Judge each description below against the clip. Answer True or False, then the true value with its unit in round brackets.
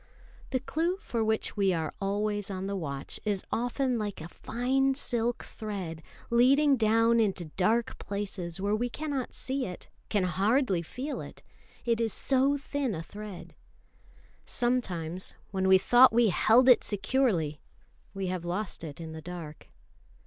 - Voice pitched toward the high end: True (215 Hz)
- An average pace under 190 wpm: True (155 wpm)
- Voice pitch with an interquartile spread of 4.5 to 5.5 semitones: True (5.1 semitones)